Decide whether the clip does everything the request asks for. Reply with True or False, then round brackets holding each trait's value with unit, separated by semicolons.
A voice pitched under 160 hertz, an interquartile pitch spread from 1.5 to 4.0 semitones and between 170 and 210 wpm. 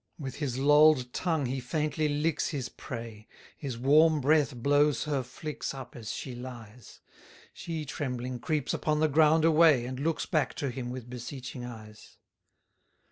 False (135 Hz; 3.6 semitones; 160 wpm)